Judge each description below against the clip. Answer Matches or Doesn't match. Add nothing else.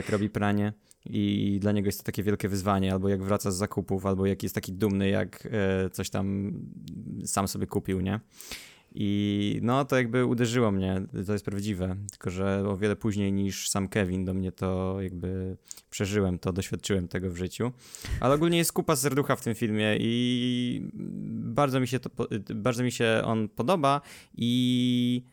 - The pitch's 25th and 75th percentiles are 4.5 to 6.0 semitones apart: Doesn't match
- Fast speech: Matches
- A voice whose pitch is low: Matches